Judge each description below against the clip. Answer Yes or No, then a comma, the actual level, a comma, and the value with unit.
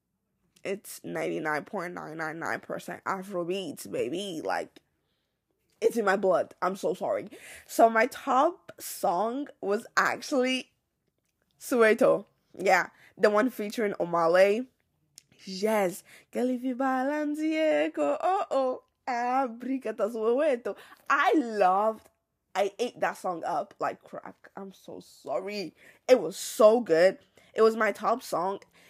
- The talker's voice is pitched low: No, high, 230 Hz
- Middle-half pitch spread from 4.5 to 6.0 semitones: Yes, average, 4.8 semitones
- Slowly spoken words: Yes, slow, 100 wpm